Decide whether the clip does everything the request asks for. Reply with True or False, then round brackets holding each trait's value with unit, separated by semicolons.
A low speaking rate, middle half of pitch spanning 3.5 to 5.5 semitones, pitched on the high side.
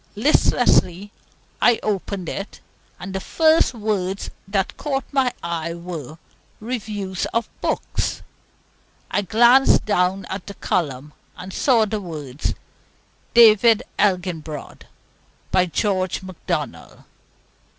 True (100 wpm; 3.8 semitones; 195 Hz)